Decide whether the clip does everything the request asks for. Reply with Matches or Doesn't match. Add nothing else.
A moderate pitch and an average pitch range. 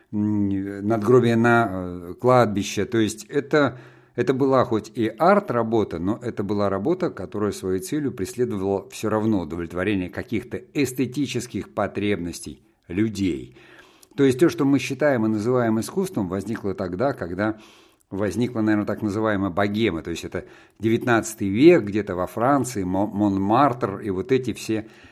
Doesn't match